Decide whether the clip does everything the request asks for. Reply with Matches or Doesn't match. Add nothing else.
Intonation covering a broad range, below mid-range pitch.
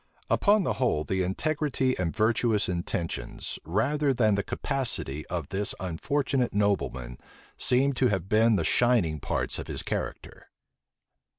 Matches